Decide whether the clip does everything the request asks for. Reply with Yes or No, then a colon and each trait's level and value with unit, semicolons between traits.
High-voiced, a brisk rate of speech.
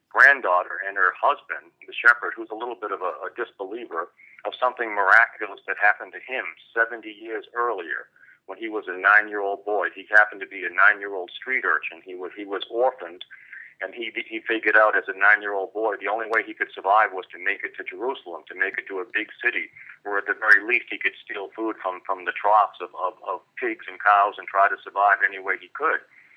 Yes: very high, 345 Hz; fast, 225 wpm